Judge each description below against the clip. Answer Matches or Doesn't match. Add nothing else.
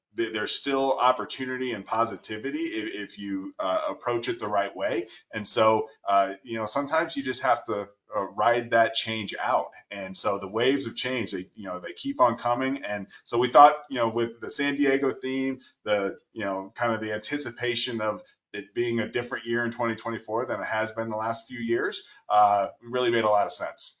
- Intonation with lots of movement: Doesn't match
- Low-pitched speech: Matches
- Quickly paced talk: Matches